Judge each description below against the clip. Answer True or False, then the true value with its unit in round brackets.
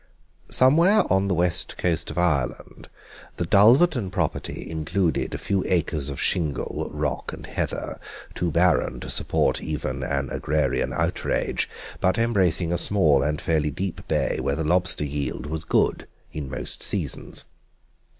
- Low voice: True (85 Hz)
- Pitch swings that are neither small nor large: True (4.3 semitones)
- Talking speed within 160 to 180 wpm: False (145 wpm)